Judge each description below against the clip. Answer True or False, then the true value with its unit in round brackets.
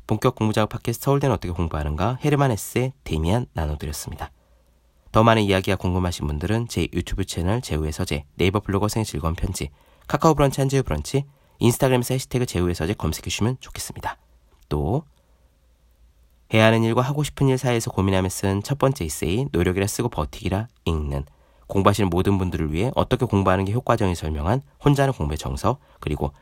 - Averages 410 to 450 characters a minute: True (440 characters per minute)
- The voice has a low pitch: True (95 Hz)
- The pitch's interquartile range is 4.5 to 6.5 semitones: False (7.6 semitones)